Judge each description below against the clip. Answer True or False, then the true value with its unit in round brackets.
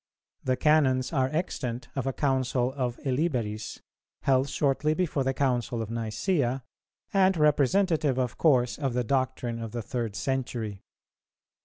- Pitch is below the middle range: True (130 Hz)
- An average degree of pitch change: True (3.0 semitones)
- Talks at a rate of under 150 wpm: True (140 wpm)